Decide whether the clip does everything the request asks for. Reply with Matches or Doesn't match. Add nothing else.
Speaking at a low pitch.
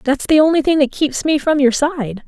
Doesn't match